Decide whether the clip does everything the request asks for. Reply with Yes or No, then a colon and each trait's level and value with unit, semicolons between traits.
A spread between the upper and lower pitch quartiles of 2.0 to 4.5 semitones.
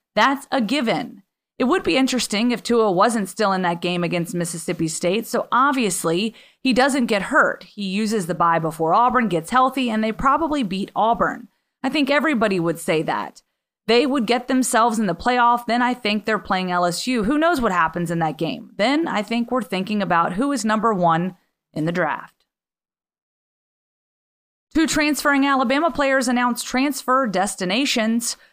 No: wide, 5.6 semitones